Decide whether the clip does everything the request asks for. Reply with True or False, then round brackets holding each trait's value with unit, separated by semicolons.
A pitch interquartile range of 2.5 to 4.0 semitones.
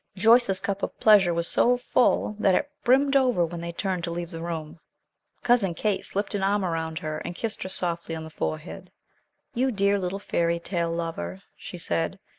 True (3.7 semitones)